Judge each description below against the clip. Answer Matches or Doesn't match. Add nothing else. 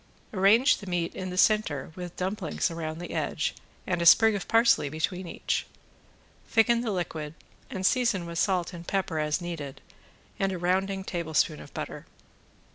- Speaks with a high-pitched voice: Doesn't match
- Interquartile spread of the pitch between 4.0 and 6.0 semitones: Doesn't match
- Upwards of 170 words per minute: Doesn't match